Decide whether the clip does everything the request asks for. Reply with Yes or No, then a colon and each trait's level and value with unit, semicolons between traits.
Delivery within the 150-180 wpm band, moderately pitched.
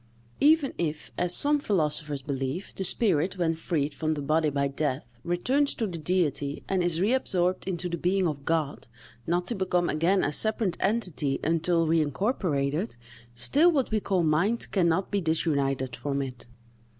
Yes: average, 165 wpm; medium, 170 Hz